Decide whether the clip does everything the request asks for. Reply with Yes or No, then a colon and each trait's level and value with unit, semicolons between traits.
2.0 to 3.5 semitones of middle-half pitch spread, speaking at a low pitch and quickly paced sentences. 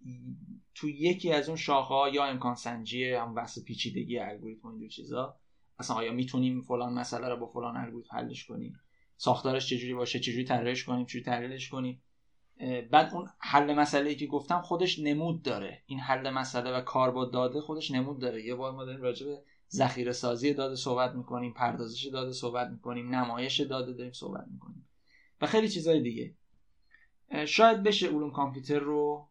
Yes: average, 2.9 semitones; low, 130 Hz; fast, 165 wpm